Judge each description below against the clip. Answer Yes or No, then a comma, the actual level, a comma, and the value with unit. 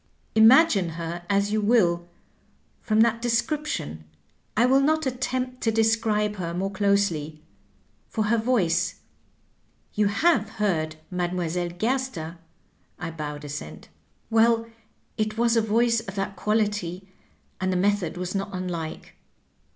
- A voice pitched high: Yes, high, 205 Hz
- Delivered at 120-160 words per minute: Yes, slow, 135 wpm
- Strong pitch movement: No, average, 4.7 semitones